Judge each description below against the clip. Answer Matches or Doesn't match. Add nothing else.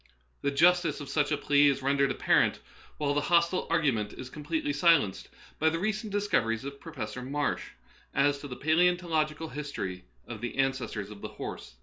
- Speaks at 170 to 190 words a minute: Matches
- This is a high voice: Doesn't match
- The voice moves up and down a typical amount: Matches